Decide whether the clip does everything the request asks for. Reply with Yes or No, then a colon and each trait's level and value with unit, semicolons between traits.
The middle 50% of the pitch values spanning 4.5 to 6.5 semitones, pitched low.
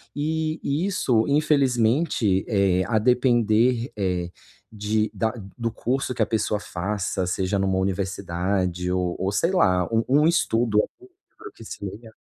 Yes: average, 5.1 semitones; low, 110 Hz